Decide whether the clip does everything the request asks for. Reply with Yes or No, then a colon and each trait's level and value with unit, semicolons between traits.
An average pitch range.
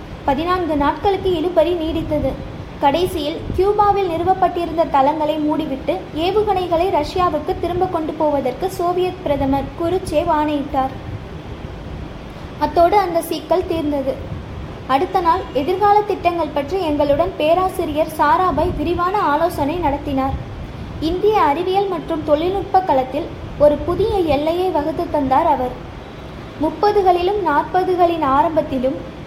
Yes: average, 3.4 semitones